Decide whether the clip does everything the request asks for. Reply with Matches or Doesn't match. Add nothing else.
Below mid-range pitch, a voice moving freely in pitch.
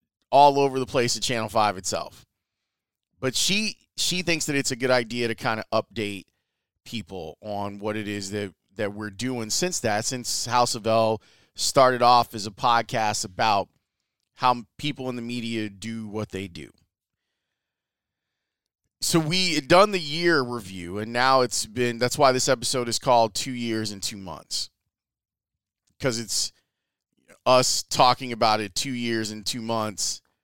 Doesn't match